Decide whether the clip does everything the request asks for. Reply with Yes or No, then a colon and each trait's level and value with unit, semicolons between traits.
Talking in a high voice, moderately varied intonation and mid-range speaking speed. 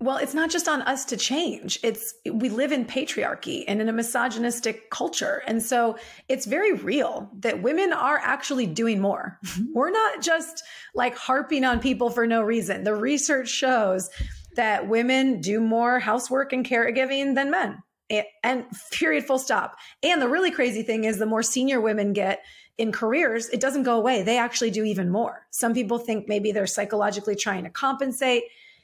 Yes: high, 240 Hz; average, 3.4 semitones; average, 180 wpm